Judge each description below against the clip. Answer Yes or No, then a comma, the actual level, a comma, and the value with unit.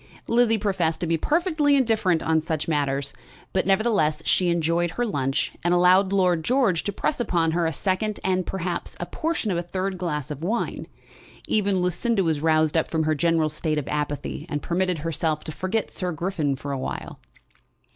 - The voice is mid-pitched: Yes, medium, 175 Hz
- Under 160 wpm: No, average, 185 wpm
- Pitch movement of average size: Yes, average, 3.8 semitones